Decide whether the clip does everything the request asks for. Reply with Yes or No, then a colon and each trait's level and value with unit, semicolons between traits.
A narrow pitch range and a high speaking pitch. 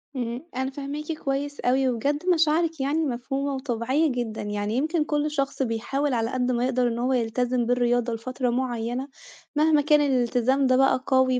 No: average, 3.0 semitones; very high, 260 Hz